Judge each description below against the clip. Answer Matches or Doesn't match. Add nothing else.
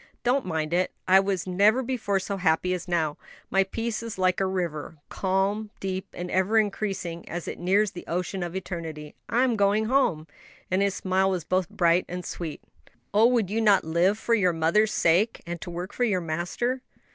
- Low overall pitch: Doesn't match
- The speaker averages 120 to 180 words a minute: Doesn't match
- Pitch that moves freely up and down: Doesn't match